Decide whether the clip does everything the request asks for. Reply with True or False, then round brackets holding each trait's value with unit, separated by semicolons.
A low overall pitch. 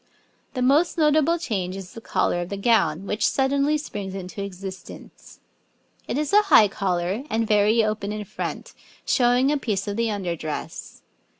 False (210 Hz)